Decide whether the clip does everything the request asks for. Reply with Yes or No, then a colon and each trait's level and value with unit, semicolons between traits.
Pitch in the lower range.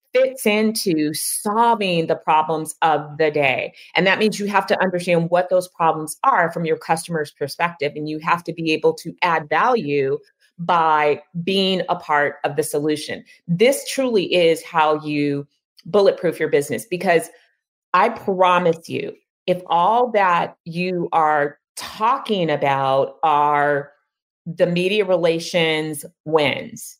No: medium, 170 Hz